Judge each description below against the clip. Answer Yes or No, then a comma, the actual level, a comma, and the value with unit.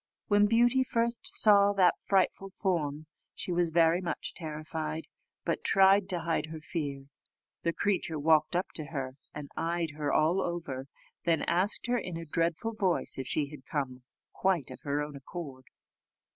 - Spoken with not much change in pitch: No, average, 4.2 semitones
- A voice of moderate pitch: Yes, medium, 165 Hz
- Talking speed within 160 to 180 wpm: Yes, average, 165 wpm